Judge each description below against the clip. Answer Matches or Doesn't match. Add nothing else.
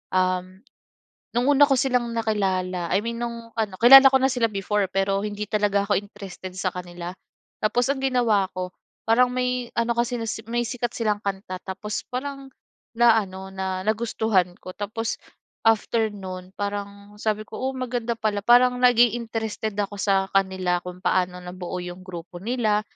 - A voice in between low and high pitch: Doesn't match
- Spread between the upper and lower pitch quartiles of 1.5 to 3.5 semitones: Doesn't match